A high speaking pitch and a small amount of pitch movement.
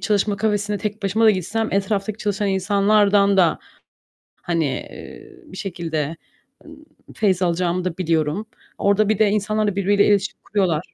Yes: high, 200 Hz; narrow, 2.3 semitones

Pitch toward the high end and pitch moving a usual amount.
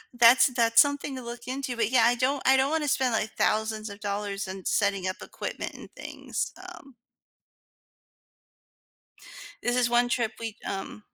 Yes: high, 235 Hz; average, 3.5 semitones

